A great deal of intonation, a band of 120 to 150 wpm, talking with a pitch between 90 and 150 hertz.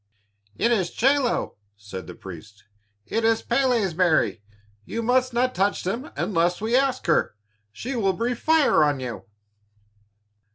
No: wide, 8.1 semitones; average, 140 wpm; high, 220 Hz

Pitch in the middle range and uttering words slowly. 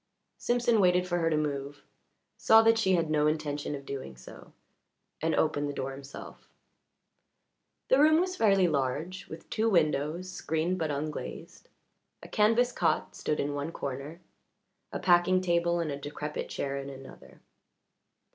No: medium, 160 Hz; average, 155 wpm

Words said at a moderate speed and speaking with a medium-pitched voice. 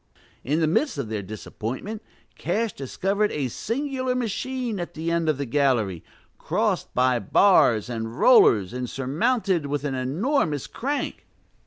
Yes: average, 145 wpm; medium, 150 Hz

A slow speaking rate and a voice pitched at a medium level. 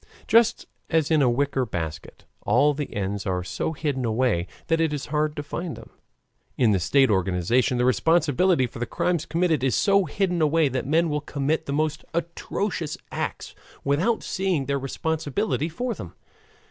No: average, 170 wpm; medium, 145 Hz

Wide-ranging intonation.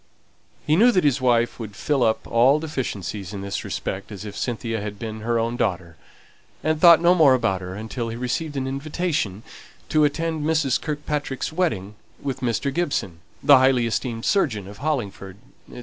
Yes: wide, 5.9 semitones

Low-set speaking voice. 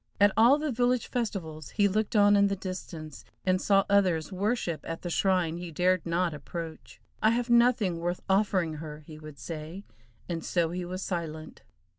No: medium, 185 Hz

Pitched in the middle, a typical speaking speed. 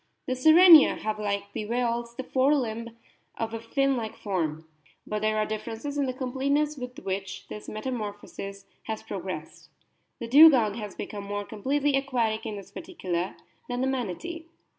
No: high, 230 Hz; average, 185 wpm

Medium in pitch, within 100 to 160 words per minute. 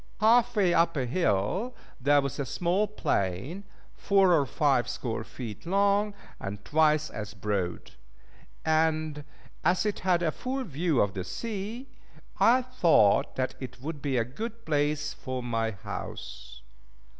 Yes: medium, 150 Hz; average, 145 wpm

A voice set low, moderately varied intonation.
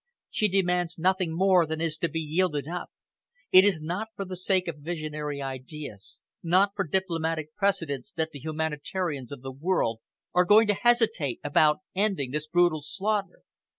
No: medium, 165 Hz; average, 3.8 semitones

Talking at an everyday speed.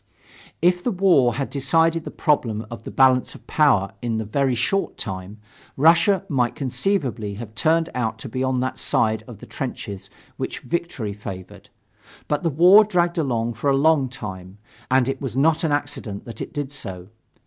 Yes: average, 180 wpm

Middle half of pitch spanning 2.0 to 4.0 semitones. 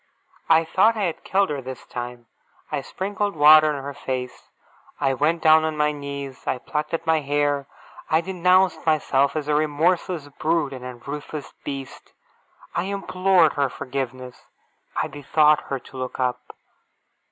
Yes: average, 3.2 semitones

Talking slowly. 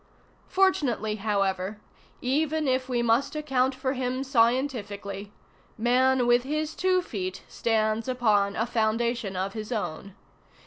Yes: slow, 125 wpm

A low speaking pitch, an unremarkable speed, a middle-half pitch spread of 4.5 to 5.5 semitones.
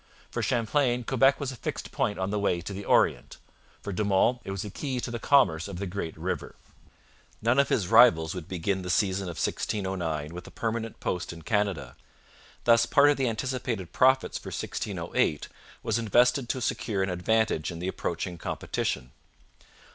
Yes: low, 105 Hz; average, 185 wpm; average, 5.1 semitones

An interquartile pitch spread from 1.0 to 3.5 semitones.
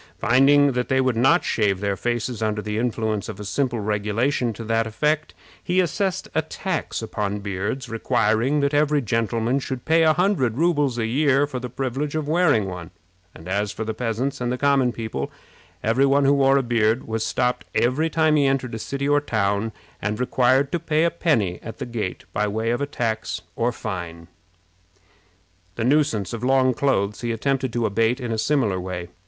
No: average, 4.3 semitones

